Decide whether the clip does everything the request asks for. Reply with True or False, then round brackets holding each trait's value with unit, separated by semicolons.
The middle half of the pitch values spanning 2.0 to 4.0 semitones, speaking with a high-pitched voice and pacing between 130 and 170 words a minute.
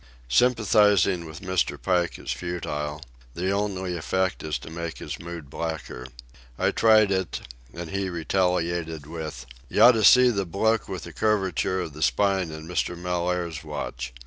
False (3.3 semitones; 90 Hz; 150 wpm)